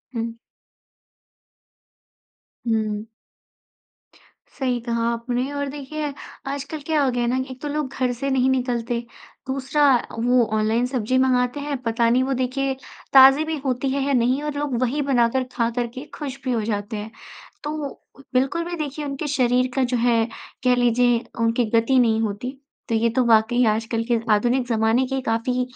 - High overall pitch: Yes, very high, 250 Hz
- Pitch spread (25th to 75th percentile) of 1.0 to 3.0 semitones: Yes, average, 2.7 semitones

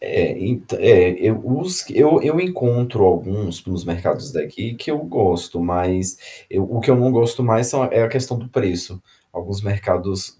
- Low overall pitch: Yes, low, 115 Hz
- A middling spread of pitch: No, wide, 5.9 semitones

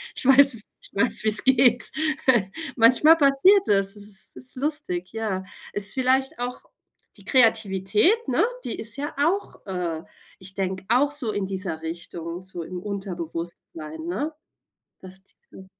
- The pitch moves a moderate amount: No, wide, 6.0 semitones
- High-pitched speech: Yes, high, 210 Hz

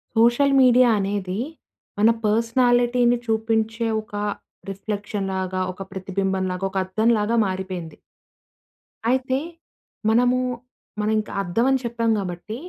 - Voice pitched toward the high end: Yes, high, 220 Hz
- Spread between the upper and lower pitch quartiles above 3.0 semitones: Yes, average, 3.7 semitones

